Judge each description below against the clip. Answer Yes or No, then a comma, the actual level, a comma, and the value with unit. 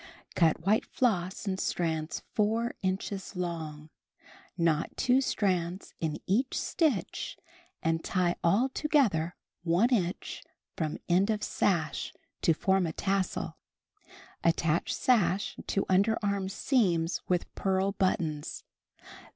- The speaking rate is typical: No, slow, 110 wpm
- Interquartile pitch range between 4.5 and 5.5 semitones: No, average, 3.6 semitones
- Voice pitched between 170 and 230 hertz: Yes, medium, 185 Hz